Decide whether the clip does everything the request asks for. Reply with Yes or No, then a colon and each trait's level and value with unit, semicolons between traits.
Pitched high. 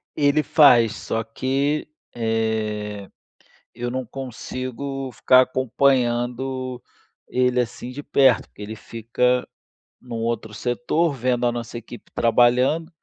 No: low, 125 Hz